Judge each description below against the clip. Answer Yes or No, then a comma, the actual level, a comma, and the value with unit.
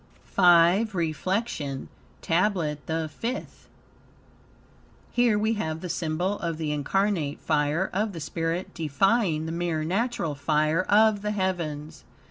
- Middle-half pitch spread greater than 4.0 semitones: Yes, average, 4.4 semitones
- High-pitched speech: No, medium, 170 Hz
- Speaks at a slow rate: Yes, slow, 120 wpm